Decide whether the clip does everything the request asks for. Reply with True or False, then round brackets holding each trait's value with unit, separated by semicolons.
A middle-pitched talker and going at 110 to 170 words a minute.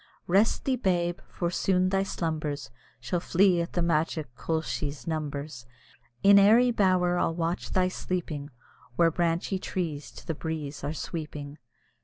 True (170 Hz; 145 wpm)